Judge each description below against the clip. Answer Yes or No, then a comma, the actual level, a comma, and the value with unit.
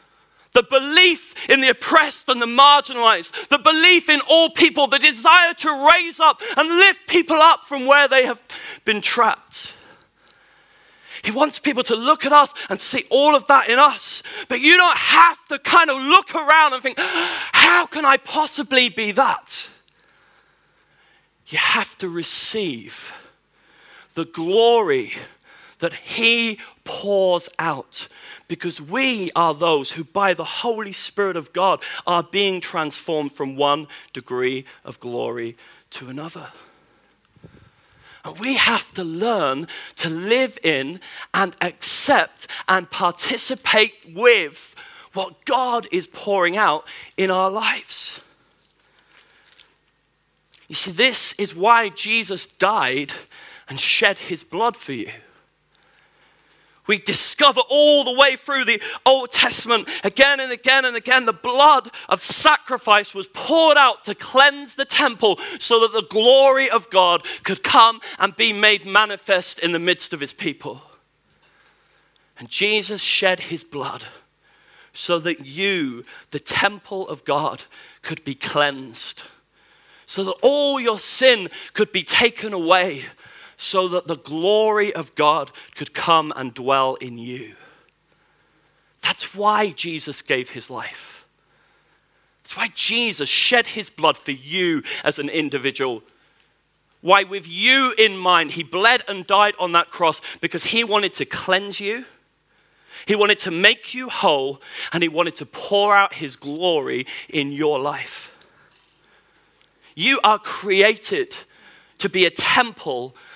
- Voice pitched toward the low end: No, high, 215 Hz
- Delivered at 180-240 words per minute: No, average, 140 wpm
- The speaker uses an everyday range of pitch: No, wide, 7.4 semitones